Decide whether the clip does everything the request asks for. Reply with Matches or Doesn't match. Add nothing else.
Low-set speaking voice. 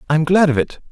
Doesn't match